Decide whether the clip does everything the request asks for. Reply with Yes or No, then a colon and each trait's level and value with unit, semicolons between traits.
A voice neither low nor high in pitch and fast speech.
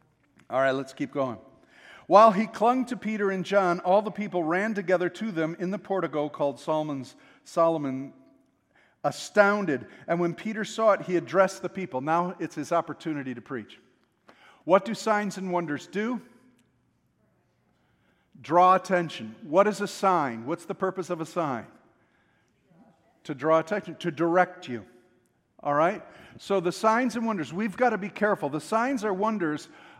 No: medium, 180 Hz; average, 160 wpm